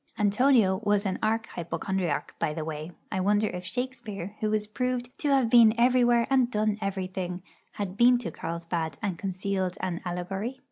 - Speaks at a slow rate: No, average, 170 wpm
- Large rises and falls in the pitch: No, average, 4.6 semitones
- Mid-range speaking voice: No, high, 205 Hz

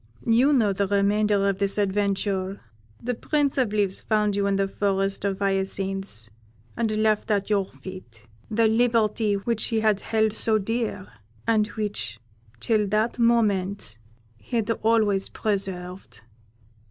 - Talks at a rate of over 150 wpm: No, average, 140 wpm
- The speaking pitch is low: No, high, 205 Hz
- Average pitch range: No, narrow, 2.1 semitones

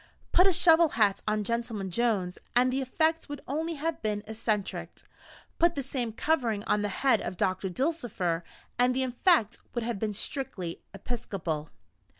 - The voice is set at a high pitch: Yes, high, 235 Hz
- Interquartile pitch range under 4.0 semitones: No, wide, 5.4 semitones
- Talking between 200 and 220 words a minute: No, average, 160 wpm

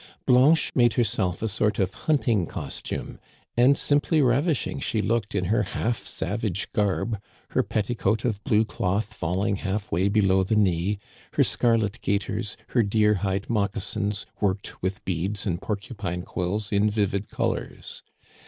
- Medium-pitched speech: No, low, 105 Hz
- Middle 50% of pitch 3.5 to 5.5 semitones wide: No, narrow, 2.6 semitones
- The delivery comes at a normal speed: Yes, average, 150 wpm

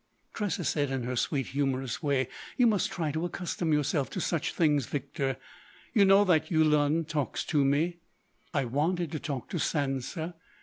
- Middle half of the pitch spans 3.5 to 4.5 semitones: Yes, average, 3.8 semitones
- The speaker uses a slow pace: No, average, 170 wpm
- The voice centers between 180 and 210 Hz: No, medium, 150 Hz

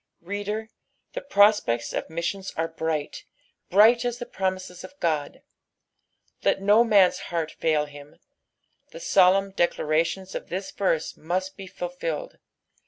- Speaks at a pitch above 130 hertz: Yes, medium, 185 Hz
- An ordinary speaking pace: No, slow, 130 wpm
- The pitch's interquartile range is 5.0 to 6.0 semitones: No, average, 3.8 semitones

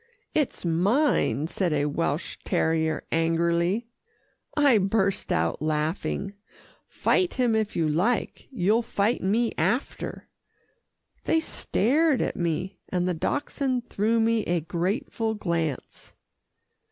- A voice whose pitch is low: No, high, 195 Hz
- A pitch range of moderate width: No, wide, 5.7 semitones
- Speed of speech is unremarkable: No, slow, 115 wpm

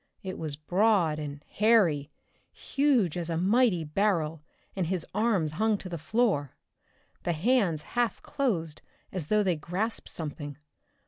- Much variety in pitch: Yes, wide, 5.8 semitones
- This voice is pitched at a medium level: Yes, medium, 180 Hz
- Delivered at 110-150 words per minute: Yes, average, 140 wpm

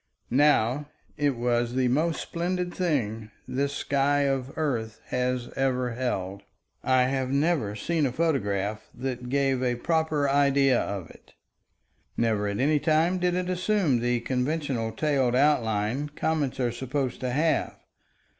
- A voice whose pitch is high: No, low, 135 Hz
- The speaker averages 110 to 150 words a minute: Yes, average, 140 wpm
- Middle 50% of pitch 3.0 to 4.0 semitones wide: Yes, average, 3.7 semitones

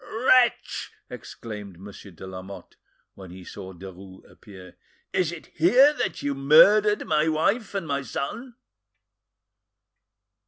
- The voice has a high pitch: No, medium, 140 Hz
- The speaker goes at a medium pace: No, slow, 120 wpm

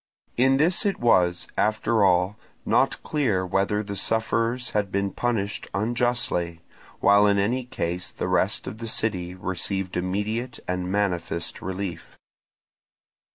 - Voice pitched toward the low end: Yes, low, 100 Hz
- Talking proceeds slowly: Yes, slow, 130 wpm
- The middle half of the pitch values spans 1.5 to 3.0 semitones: No, average, 4.1 semitones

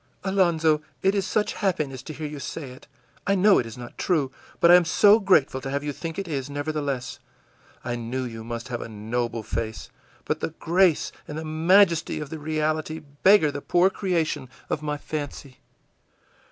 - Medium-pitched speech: Yes, medium, 150 Hz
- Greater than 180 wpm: Yes, average, 190 wpm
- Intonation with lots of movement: No, average, 4.8 semitones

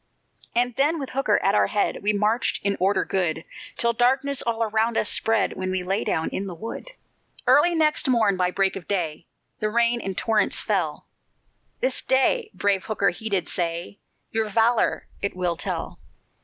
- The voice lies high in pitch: Yes, high, 210 Hz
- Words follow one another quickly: No, average, 180 wpm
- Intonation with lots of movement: No, average, 3.9 semitones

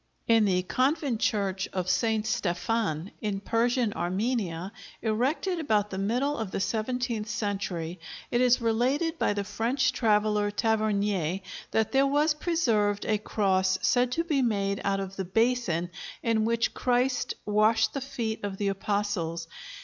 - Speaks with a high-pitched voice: Yes, high, 215 Hz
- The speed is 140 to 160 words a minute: Yes, average, 150 wpm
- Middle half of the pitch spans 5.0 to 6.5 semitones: No, average, 3.8 semitones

